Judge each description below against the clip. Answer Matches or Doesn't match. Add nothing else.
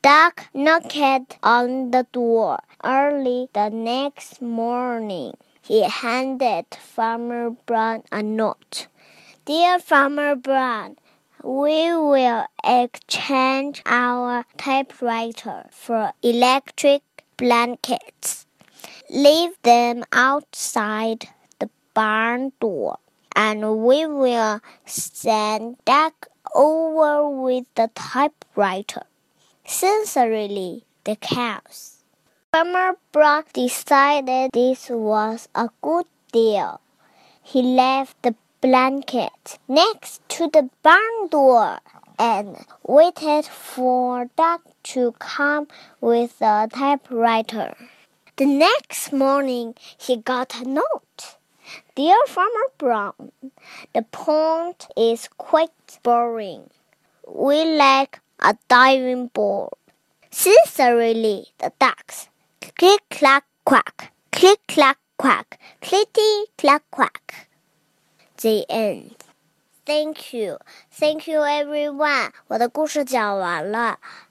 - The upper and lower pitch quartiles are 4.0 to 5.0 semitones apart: Matches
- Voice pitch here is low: Doesn't match